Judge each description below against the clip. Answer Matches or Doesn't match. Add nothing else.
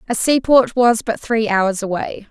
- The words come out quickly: Doesn't match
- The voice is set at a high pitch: Matches